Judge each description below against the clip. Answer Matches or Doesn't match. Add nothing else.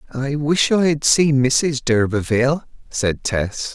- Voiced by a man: Matches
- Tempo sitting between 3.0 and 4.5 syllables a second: Matches